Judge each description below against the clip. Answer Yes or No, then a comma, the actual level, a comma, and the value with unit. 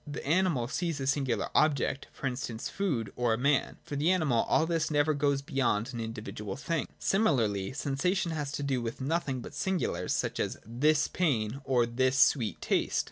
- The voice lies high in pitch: No, medium, 140 Hz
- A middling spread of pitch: Yes, average, 4.4 semitones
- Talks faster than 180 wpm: Yes, average, 190 wpm